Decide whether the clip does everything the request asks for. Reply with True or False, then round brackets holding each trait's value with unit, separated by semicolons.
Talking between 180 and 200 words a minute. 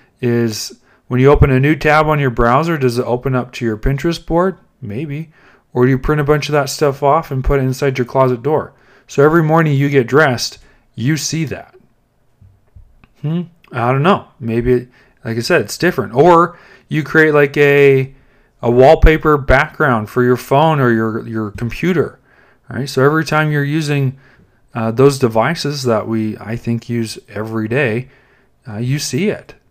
True (185 wpm)